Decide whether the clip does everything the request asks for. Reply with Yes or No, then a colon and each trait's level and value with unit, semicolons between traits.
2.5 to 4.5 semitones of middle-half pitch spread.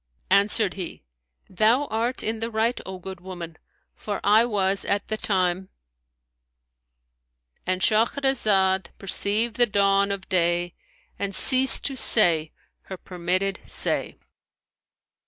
Yes: average, 4.0 semitones